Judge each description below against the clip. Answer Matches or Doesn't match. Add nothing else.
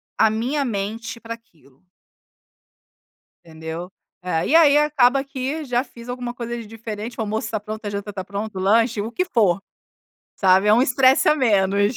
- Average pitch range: Matches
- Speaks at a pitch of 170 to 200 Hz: Doesn't match